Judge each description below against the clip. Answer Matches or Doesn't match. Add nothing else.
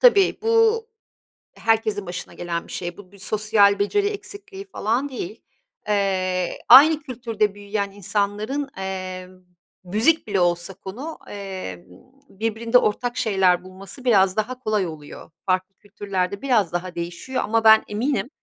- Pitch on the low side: Doesn't match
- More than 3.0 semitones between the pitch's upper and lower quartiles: Matches